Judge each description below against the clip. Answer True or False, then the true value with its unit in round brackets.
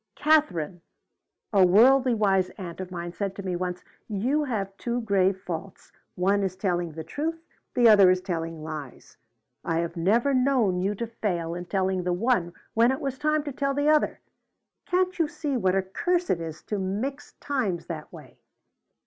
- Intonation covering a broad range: True (6.5 semitones)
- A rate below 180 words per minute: False (185 wpm)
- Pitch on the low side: False (195 Hz)